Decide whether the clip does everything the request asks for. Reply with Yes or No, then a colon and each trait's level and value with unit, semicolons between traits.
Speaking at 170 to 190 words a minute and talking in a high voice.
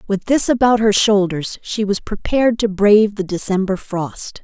Yes: average, 175 wpm; high, 205 Hz